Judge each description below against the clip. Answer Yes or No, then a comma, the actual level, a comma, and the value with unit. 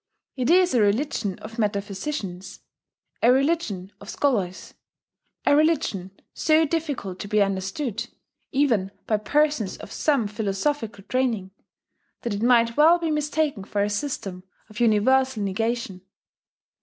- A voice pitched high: Yes, high, 230 Hz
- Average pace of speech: No, slow, 130 wpm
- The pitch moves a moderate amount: No, wide, 6.3 semitones